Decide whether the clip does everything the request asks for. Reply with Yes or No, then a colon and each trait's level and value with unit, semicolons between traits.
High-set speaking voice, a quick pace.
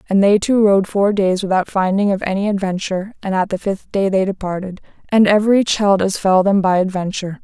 Yes: high, 195 Hz; fast, 210 wpm